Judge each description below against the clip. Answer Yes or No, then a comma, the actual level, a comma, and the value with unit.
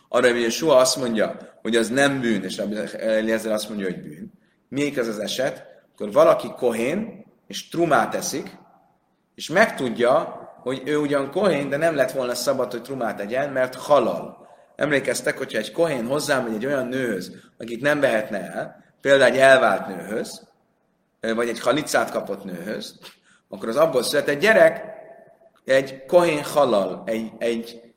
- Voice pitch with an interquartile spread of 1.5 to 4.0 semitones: No, average, 4.4 semitones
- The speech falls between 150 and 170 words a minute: Yes, fast, 155 wpm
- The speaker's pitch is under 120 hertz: No, low, 130 Hz